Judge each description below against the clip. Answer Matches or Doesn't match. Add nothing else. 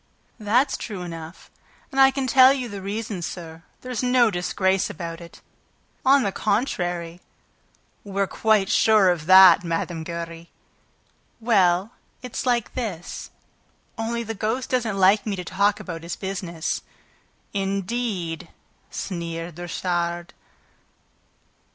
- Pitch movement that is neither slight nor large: Matches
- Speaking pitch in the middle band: Doesn't match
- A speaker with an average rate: Doesn't match